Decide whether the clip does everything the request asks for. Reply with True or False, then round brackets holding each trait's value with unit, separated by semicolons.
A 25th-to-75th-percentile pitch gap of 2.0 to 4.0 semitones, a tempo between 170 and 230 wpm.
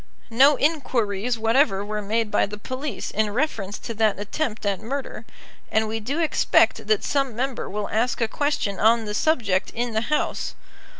False (4.4 semitones; 175 wpm)